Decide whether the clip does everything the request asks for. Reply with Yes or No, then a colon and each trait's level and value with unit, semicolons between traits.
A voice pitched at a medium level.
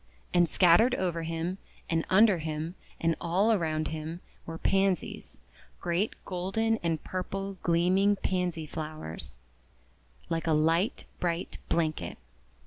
Yes: medium, 170 Hz